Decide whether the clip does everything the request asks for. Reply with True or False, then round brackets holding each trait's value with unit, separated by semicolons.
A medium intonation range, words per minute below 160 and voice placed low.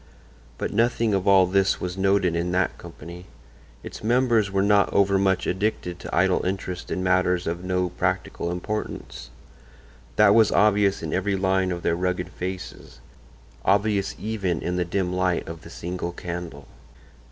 False (2.0 semitones; 150 wpm; 95 Hz)